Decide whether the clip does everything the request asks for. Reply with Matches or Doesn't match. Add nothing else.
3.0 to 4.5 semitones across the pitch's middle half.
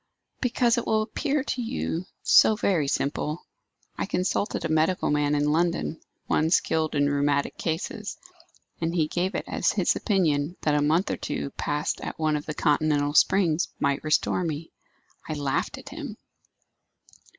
Matches